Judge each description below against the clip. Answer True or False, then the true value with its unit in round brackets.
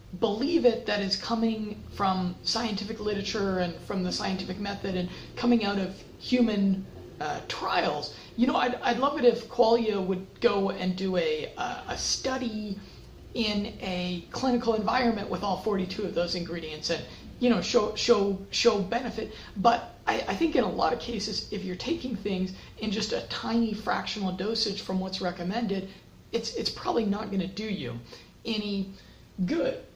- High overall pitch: True (205 Hz)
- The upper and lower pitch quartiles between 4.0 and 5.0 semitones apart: False (3.6 semitones)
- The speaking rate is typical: True (170 wpm)